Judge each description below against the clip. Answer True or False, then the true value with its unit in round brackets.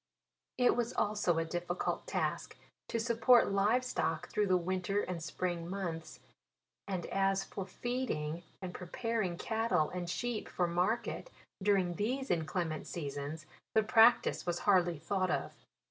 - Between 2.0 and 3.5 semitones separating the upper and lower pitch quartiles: False (4.2 semitones)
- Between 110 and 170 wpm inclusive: True (140 wpm)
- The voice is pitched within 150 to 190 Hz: True (185 Hz)